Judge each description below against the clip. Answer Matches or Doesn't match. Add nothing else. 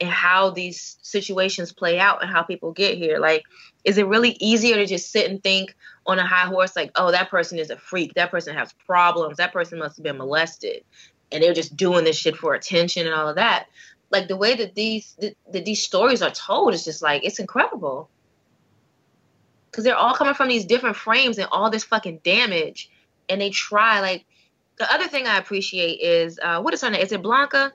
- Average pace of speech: Doesn't match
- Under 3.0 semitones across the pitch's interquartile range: Doesn't match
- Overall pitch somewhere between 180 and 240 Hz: Matches